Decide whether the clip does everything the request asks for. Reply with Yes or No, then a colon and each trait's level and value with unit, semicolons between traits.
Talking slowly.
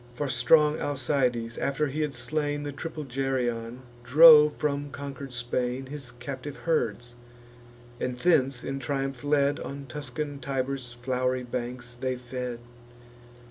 Yes: slow, 130 wpm